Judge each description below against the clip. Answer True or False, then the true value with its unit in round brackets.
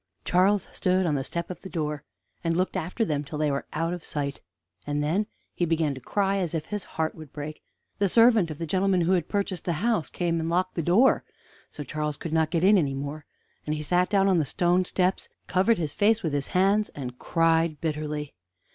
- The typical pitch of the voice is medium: True (165 Hz)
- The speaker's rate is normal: False (225 wpm)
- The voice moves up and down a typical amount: True (3.7 semitones)